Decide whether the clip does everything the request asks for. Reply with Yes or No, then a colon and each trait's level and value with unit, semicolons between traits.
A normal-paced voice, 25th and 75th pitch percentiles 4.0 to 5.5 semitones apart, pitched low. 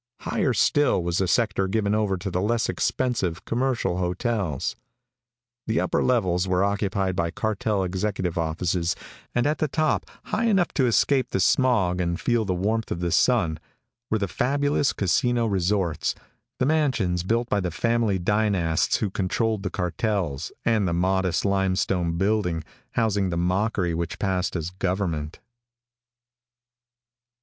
Yes: average, 145 wpm; average, 4.3 semitones; very low, 95 Hz